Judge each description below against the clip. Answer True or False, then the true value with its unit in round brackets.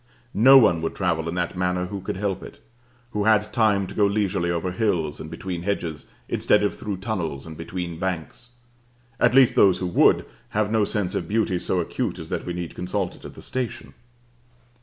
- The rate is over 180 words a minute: True (200 wpm)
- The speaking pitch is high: False (95 Hz)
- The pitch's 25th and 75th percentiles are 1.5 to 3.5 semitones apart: True (3.2 semitones)